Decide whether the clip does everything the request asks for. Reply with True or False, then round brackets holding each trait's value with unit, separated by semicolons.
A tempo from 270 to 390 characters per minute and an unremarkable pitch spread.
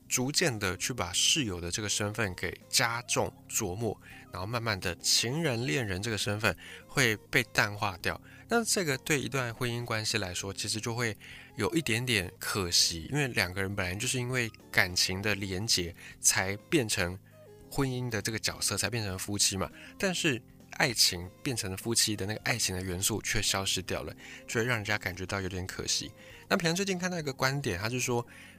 True (285 characters per minute; 5.0 semitones)